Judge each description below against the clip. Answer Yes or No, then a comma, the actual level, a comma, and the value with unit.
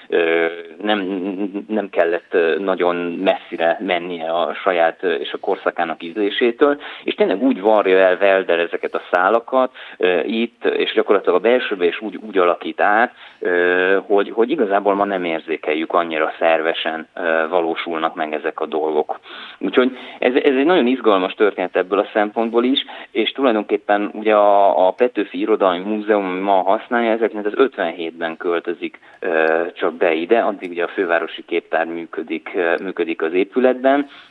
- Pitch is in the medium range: No, low, 100 Hz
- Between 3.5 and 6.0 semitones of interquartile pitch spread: Yes, average, 5.2 semitones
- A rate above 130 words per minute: Yes, average, 145 wpm